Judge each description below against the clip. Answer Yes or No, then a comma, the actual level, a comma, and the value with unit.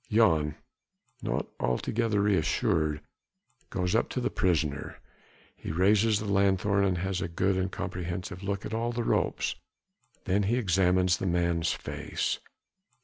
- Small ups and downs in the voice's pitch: No, average, 3.0 semitones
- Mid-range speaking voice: No, very low, 95 Hz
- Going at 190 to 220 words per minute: No, average, 145 wpm